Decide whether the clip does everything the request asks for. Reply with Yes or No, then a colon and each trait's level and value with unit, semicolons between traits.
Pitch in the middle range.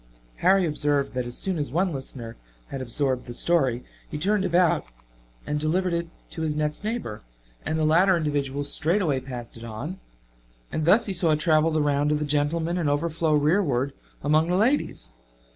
Yes: medium, 155 Hz